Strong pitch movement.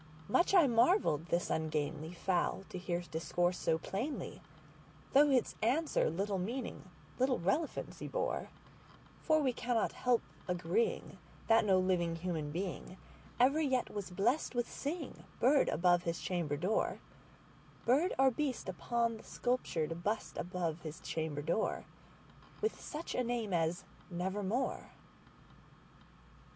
Yes: wide, 6.7 semitones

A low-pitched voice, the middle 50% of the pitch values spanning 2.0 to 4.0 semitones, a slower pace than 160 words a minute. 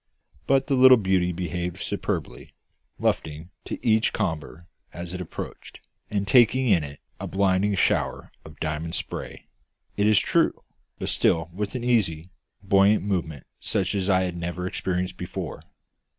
Yes: very low, 95 Hz; average, 3.4 semitones; average, 150 wpm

